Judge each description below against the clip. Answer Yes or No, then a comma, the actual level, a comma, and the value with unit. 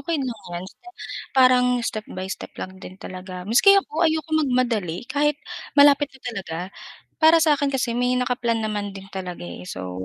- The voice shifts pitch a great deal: Yes, wide, 7.1 semitones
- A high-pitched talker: Yes, high, 240 Hz